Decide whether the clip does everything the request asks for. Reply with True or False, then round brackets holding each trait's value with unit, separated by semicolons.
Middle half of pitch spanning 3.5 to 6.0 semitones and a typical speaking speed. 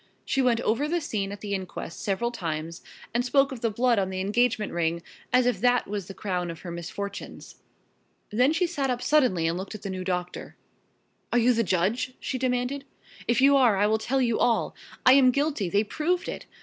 False (5.1 semitones; 215 wpm)